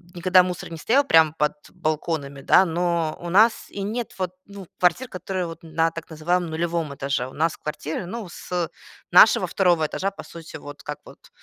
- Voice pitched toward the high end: No, medium, 170 Hz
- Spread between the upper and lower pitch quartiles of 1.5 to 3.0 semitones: Yes, average, 2.7 semitones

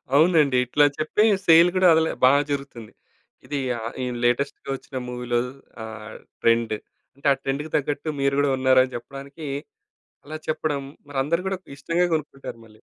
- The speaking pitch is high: No, medium, 140 Hz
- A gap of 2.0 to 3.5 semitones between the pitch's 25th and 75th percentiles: No, average, 3.9 semitones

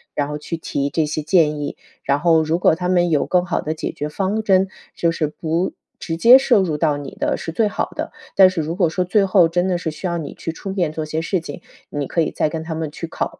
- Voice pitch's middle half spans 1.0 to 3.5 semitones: Yes, average, 2.9 semitones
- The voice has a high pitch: No, medium, 165 Hz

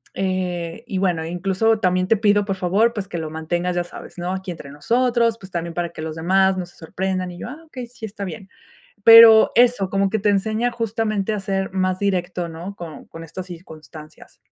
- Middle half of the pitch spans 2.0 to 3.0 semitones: No, average, 3.5 semitones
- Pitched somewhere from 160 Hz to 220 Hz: Yes, high, 190 Hz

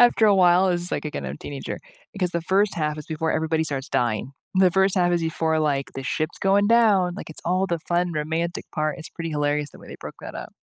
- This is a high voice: No, medium, 165 Hz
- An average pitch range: Yes, average, 3.3 semitones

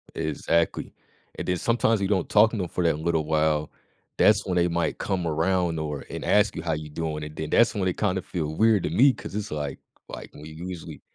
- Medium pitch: No, very low, 85 Hz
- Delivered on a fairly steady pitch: No, average, 3.9 semitones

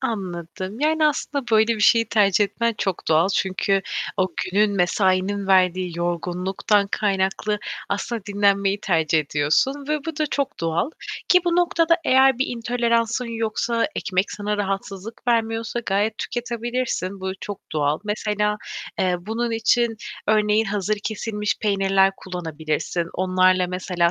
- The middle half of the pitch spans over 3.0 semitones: Yes, average, 3.7 semitones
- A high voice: Yes, high, 205 Hz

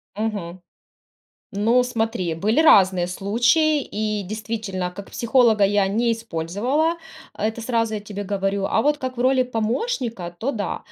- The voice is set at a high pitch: Yes, high, 220 Hz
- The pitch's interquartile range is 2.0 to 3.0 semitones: No, average, 3.6 semitones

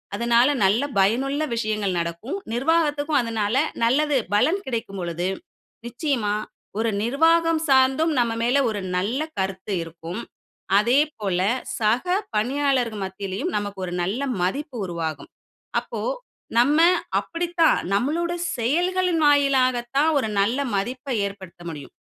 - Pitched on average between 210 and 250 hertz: Yes, high, 240 Hz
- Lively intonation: Yes, wide, 6.4 semitones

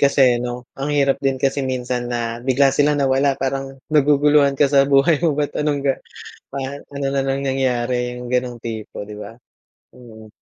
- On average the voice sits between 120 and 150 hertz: Yes, low, 135 Hz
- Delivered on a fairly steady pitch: Yes, narrow, 2.2 semitones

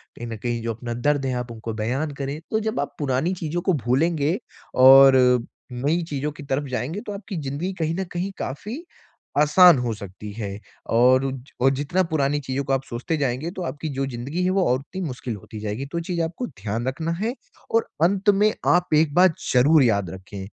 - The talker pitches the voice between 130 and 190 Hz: Yes, medium, 140 Hz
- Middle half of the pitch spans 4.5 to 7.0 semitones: Yes, wide, 5.5 semitones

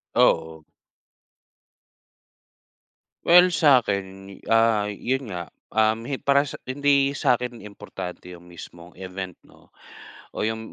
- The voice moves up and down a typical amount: No, wide, 6.9 semitones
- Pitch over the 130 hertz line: No, low, 110 Hz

